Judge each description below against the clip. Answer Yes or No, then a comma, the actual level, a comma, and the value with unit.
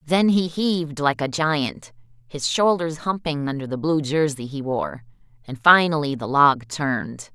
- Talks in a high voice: No, medium, 145 Hz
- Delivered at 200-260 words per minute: No, average, 165 wpm